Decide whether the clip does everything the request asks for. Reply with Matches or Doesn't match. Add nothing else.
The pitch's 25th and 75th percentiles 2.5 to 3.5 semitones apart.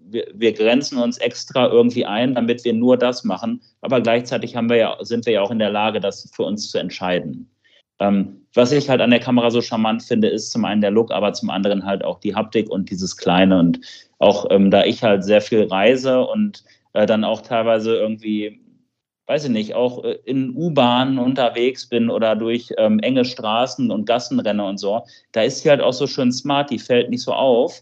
Matches